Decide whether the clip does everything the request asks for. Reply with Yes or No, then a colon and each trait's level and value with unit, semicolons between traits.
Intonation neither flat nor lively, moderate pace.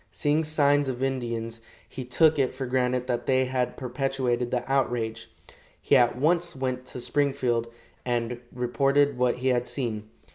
No: narrow, 2.1 semitones; average, 155 wpm